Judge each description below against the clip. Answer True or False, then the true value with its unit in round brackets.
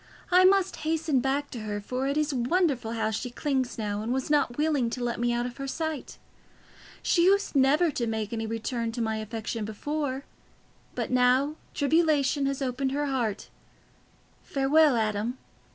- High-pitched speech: True (265 Hz)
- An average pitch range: True (4.3 semitones)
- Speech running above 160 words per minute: True (170 wpm)